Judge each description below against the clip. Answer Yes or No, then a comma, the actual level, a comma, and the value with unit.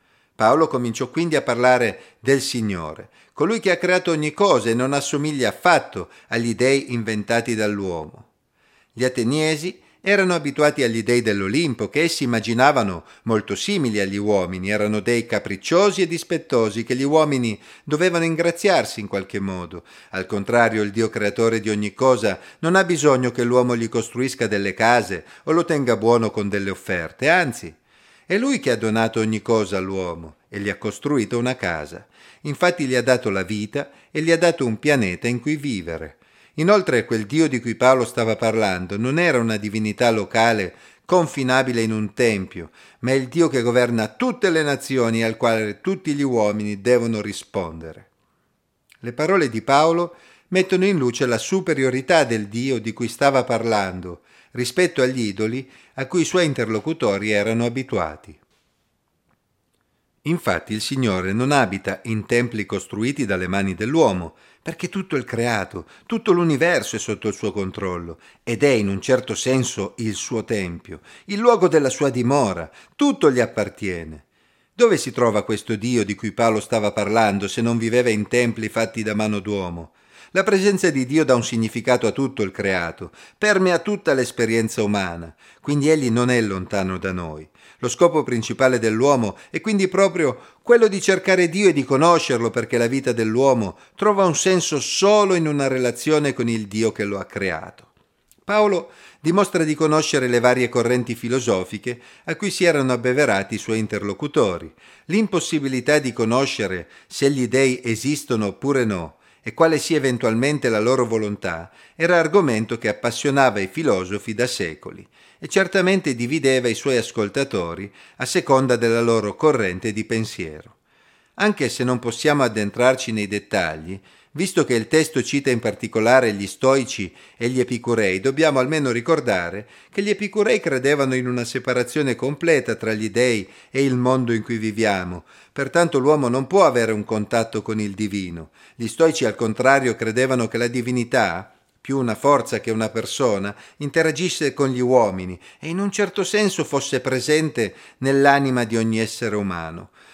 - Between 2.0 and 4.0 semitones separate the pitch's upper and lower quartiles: No, average, 5.1 semitones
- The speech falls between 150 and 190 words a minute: Yes, average, 160 wpm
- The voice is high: No, low, 120 Hz